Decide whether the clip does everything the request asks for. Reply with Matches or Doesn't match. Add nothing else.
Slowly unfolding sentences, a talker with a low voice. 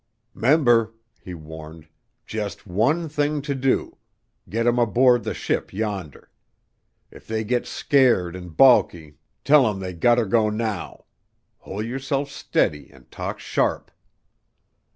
Matches